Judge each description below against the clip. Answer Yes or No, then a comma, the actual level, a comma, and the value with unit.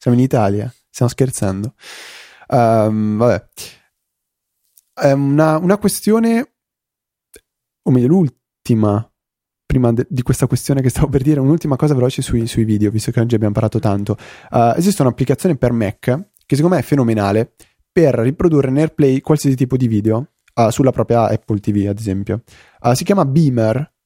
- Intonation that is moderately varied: Yes, average, 4.5 semitones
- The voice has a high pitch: No, low, 125 Hz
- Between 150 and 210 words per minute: Yes, average, 155 wpm